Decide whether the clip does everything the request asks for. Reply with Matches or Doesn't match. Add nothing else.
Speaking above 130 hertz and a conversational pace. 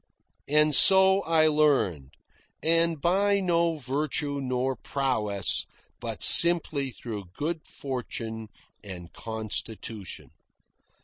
Doesn't match